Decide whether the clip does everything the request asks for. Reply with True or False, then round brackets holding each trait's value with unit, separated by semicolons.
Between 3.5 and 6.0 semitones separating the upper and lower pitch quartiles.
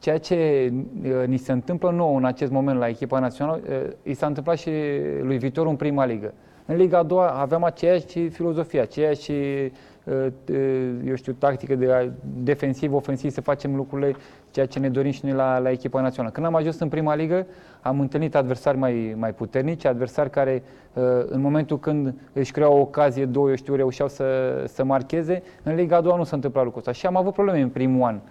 False (2.9 semitones)